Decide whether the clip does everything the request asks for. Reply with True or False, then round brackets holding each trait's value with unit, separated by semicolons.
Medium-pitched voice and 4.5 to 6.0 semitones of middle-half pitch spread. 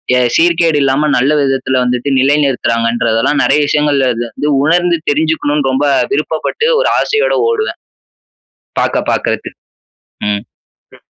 False (145 Hz; 3.8 semitones)